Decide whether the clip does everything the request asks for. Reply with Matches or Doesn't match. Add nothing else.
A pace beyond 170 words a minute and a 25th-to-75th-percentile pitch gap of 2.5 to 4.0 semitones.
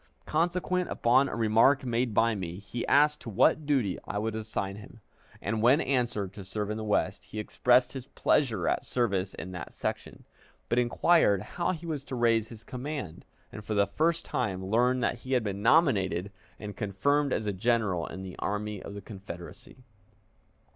Doesn't match